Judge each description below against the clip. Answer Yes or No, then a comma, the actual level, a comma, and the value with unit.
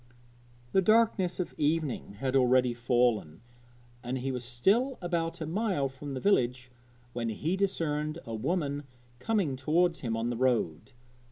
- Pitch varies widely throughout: Yes, wide, 6.1 semitones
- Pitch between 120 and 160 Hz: Yes, medium, 140 Hz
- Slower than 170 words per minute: Yes, average, 150 wpm